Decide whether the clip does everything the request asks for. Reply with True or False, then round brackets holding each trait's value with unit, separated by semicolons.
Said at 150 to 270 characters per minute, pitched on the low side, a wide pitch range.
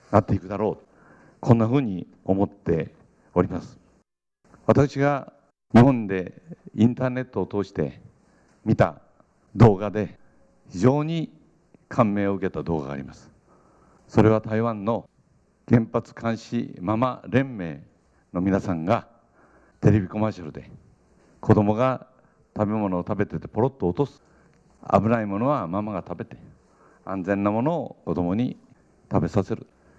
False (260 characters per minute; 105 Hz; 3.9 semitones)